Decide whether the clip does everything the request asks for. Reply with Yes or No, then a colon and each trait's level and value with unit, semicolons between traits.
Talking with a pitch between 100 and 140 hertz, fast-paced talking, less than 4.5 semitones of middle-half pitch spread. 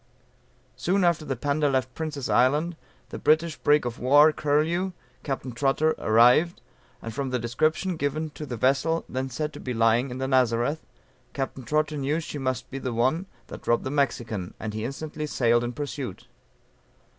No: low, 135 Hz; average, 175 wpm; average, 3.8 semitones